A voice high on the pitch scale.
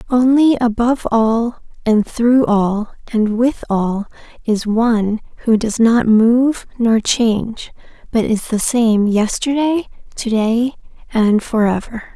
Yes: high, 230 Hz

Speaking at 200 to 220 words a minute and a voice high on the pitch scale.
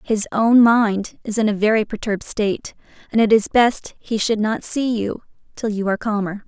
Yes: fast, 205 wpm; high, 215 Hz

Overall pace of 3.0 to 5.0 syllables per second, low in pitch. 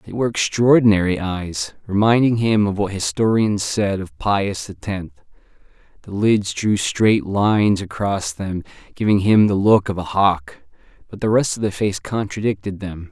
Yes: 4.6 syllables/s; low, 100 Hz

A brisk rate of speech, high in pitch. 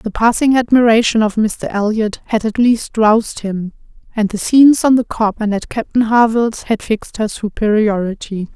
No: average, 175 wpm; high, 220 Hz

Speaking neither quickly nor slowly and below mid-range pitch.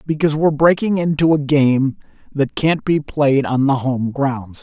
No: average, 180 wpm; medium, 145 Hz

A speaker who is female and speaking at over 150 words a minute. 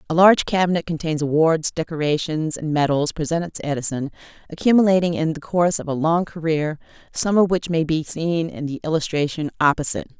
Yes: female; average, 170 wpm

